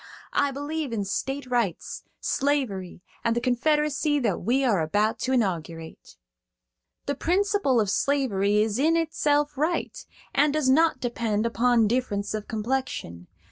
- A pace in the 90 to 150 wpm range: Yes, average, 140 wpm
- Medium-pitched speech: No, very high, 250 Hz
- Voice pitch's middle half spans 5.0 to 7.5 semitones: Yes, wide, 5.5 semitones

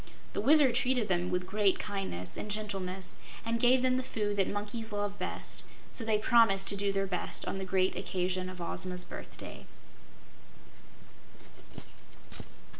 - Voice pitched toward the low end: No, high, 200 Hz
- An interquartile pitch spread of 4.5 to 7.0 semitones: No, average, 3.2 semitones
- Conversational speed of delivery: Yes, average, 150 wpm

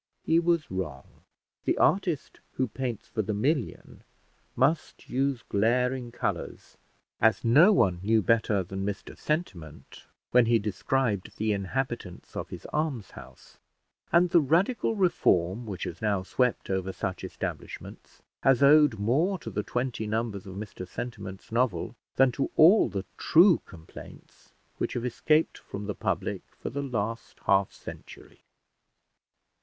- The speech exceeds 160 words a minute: No, average, 140 wpm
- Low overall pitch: Yes, low, 115 Hz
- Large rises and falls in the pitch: Yes, wide, 5.8 semitones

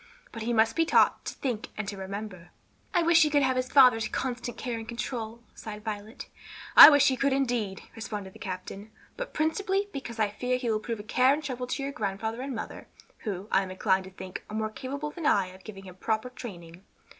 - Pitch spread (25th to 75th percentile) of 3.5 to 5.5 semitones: Yes, average, 4.4 semitones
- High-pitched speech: Yes, high, 225 Hz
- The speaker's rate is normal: No, fast, 225 wpm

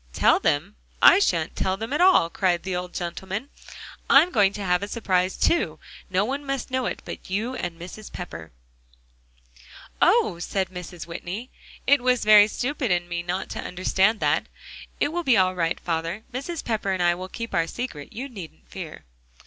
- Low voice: No, high, 190 Hz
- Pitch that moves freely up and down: Yes, wide, 5.7 semitones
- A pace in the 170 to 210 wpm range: Yes, average, 185 wpm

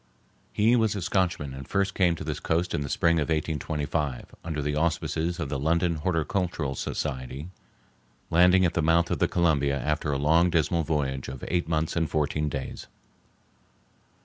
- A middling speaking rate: Yes, average, 175 wpm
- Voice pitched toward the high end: No, very low, 80 Hz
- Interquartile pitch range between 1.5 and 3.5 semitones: Yes, average, 2.9 semitones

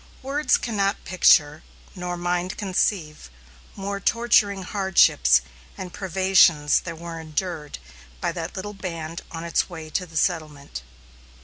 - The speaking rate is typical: No, slow, 125 wpm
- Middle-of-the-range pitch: Yes, medium, 175 Hz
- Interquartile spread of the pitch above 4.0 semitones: No, average, 3.4 semitones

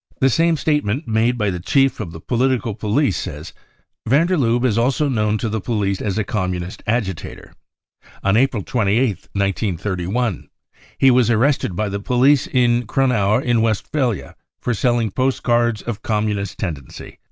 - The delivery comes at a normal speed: Yes, average, 165 wpm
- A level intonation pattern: No, average, 4.0 semitones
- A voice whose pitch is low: Yes, low, 115 Hz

